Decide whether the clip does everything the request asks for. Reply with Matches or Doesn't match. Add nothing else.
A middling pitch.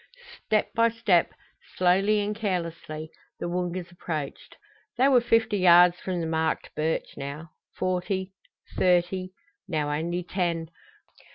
Matches